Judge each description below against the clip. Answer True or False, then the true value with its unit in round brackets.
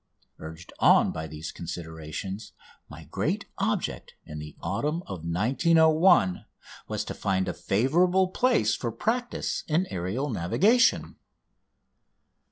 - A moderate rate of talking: False (115 wpm)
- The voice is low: True (105 Hz)